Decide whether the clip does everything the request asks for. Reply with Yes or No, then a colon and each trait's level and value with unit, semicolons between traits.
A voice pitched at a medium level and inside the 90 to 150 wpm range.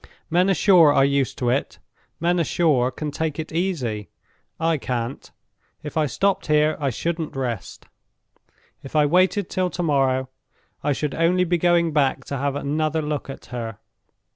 No: medium, 150 Hz; average, 165 wpm